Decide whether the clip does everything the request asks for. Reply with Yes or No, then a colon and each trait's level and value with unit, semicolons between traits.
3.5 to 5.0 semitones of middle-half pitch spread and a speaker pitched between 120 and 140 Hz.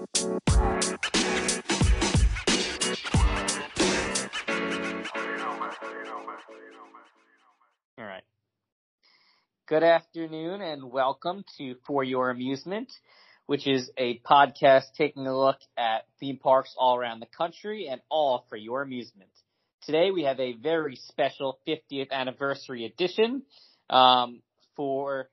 Yes: average, 4.1 semitones; low, 135 Hz